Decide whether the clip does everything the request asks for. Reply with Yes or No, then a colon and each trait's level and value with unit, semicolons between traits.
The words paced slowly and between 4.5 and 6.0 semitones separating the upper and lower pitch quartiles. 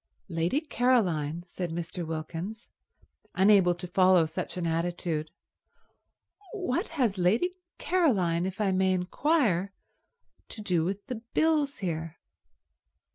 Yes: slow, 115 wpm; wide, 5.5 semitones